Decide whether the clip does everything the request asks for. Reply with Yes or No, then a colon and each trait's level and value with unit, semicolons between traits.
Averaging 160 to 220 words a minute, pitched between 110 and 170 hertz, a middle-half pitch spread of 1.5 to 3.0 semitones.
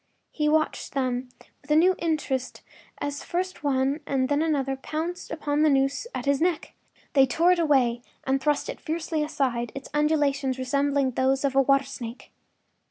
No: average, 175 wpm; very high, 280 Hz; narrow, 2.5 semitones